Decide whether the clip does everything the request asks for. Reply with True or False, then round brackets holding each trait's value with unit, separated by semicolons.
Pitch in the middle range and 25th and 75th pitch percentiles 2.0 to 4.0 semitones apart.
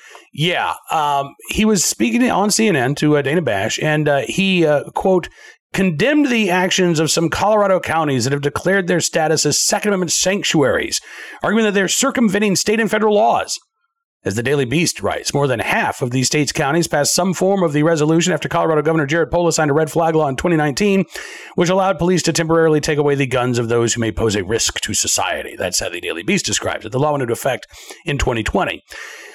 False (165 Hz; 5.1 semitones)